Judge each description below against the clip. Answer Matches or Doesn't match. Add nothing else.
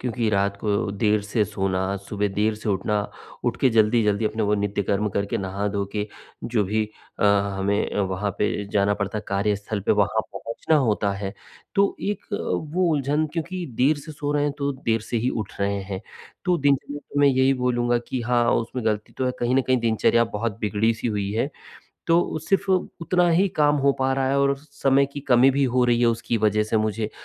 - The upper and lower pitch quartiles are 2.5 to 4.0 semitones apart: Doesn't match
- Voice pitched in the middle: Doesn't match